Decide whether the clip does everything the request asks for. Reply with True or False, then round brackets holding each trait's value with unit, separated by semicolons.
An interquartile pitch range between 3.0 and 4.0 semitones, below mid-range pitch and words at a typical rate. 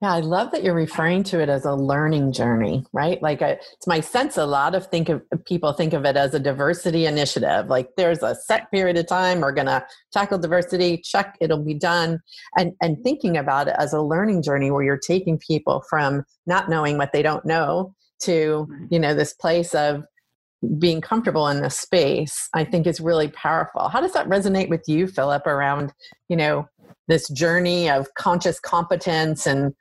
False (3.3 semitones; 165 Hz; 195 wpm)